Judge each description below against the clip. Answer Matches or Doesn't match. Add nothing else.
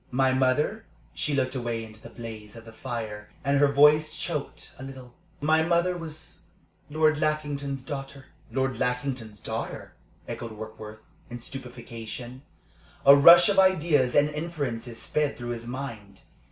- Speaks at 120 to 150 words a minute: Matches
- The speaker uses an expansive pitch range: Doesn't match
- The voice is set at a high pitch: Doesn't match